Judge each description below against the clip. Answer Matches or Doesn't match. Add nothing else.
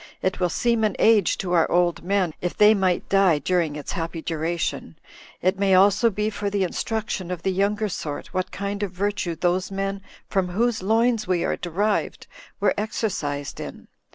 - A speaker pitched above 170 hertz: Matches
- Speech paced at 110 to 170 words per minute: Doesn't match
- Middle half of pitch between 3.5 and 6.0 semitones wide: Doesn't match